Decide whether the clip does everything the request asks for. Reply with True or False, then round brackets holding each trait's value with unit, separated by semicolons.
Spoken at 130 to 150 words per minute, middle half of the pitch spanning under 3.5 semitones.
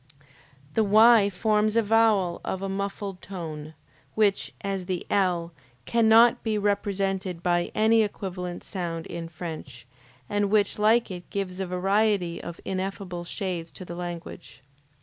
True (140 wpm; 3.1 semitones)